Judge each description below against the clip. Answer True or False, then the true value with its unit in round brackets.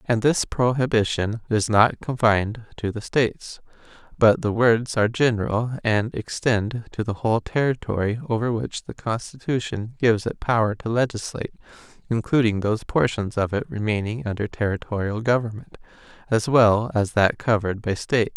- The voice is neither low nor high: False (115 Hz)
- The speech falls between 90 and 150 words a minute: True (145 wpm)